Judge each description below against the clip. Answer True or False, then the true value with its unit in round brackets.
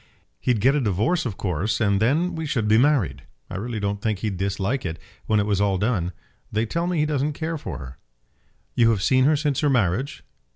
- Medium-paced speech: False (220 wpm)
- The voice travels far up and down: True (6.2 semitones)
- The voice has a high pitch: False (110 Hz)